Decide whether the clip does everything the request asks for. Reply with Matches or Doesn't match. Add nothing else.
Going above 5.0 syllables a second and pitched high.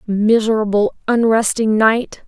Doesn't match